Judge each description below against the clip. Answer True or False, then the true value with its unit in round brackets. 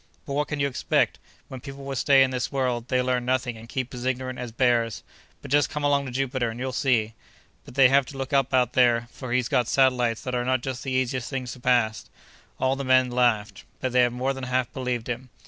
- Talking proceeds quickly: True (240 wpm)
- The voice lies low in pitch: True (130 Hz)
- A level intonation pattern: True (1.5 semitones)